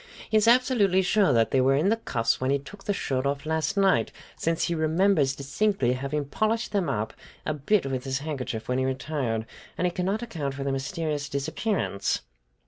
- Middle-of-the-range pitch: Yes, medium, 150 Hz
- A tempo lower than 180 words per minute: No, average, 200 wpm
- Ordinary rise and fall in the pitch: No, wide, 6.5 semitones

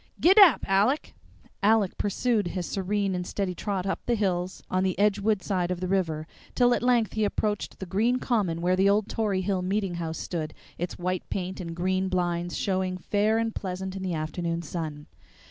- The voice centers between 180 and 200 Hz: Yes, high, 190 Hz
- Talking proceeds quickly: No, average, 195 wpm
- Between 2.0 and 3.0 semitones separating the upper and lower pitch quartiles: Yes, average, 2.7 semitones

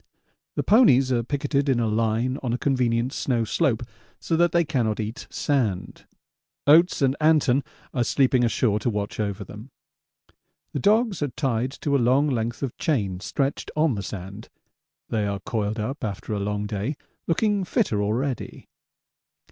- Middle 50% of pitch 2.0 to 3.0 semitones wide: No, average, 4.8 semitones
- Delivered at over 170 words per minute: No, average, 165 wpm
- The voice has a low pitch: Yes, low, 125 Hz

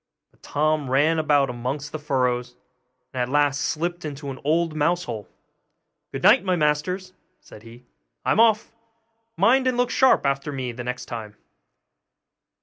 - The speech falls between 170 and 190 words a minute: No, average, 155 wpm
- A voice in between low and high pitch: Yes, medium, 145 Hz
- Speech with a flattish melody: No, average, 5.1 semitones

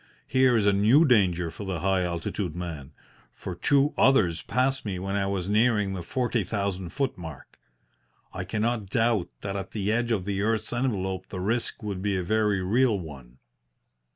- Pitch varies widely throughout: No, average, 3.7 semitones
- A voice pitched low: Yes, low, 100 Hz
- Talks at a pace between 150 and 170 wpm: No, average, 180 wpm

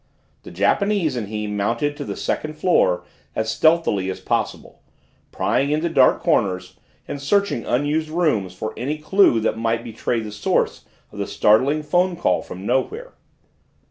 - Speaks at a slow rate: No, average, 155 wpm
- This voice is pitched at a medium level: No, low, 130 Hz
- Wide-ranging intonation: Yes, wide, 6.7 semitones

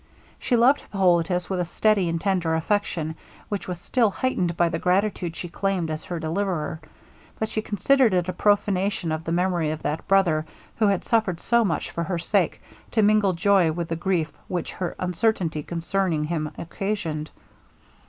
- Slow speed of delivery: No, average, 175 wpm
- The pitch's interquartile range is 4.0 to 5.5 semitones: No, average, 3.5 semitones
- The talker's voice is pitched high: No, medium, 180 Hz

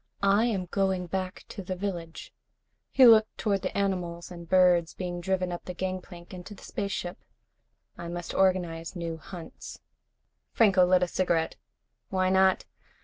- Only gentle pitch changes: Yes, narrow, 1.8 semitones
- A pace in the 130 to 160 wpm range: Yes, average, 150 wpm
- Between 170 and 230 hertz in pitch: Yes, medium, 185 Hz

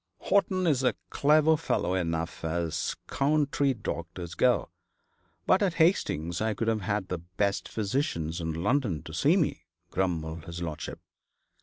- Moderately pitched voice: No, low, 100 Hz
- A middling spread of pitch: No, wide, 9.0 semitones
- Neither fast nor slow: Yes, average, 145 wpm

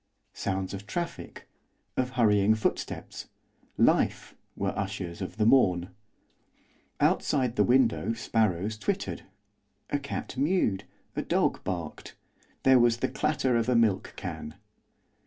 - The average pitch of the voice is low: Yes, low, 110 Hz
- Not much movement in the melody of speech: No, average, 4.6 semitones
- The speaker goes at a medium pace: No, slow, 120 wpm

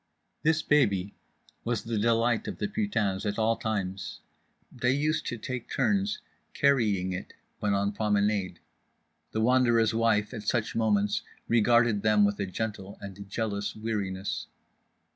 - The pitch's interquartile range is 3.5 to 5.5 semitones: No, average, 2.9 semitones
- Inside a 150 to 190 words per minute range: No, average, 140 wpm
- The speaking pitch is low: Yes, low, 110 Hz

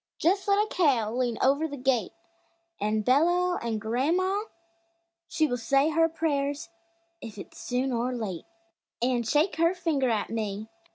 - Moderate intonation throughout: No, wide, 6.0 semitones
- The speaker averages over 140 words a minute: Yes, average, 155 wpm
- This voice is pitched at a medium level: No, very high, 270 Hz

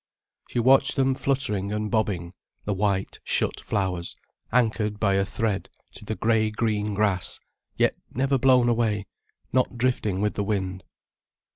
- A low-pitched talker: Yes, low, 105 Hz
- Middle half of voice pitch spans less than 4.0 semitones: Yes, average, 3.3 semitones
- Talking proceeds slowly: No, average, 145 wpm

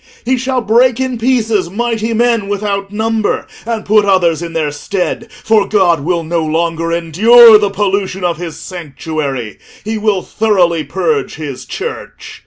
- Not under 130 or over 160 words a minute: Yes, average, 155 wpm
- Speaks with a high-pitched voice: Yes, high, 200 Hz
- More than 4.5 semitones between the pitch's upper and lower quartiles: Yes, average, 5.0 semitones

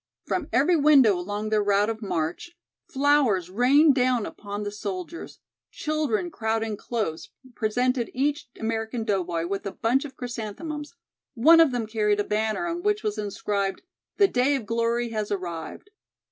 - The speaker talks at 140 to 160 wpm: Yes, average, 155 wpm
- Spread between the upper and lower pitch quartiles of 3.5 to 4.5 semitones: No, average, 5.2 semitones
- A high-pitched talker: Yes, high, 225 Hz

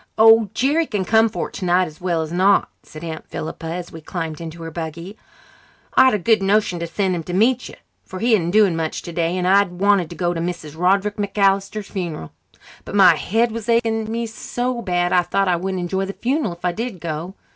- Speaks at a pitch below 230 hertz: Yes, medium, 185 Hz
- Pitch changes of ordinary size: Yes, average, 3.9 semitones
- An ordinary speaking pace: No, fast, 220 wpm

